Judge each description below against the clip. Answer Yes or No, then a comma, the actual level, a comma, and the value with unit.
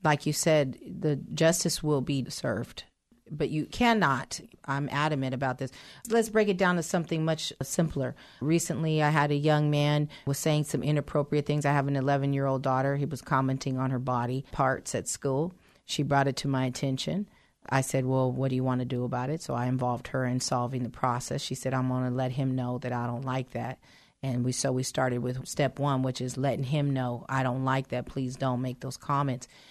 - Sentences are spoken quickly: Yes, fast, 220 wpm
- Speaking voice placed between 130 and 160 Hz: Yes, low, 135 Hz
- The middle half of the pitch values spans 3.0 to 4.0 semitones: No, narrow, 2.6 semitones